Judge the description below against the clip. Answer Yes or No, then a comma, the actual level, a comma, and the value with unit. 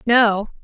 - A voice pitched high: Yes, high, 220 Hz